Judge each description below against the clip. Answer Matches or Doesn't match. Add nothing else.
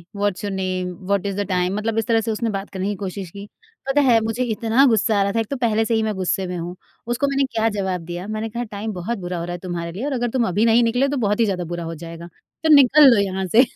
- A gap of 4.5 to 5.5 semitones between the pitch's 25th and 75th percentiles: Doesn't match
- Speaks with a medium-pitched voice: Doesn't match